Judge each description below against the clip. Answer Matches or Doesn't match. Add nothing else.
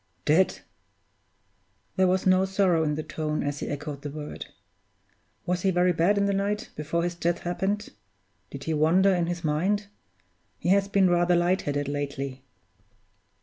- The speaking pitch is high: Doesn't match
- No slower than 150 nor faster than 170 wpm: Matches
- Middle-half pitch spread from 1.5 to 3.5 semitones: Doesn't match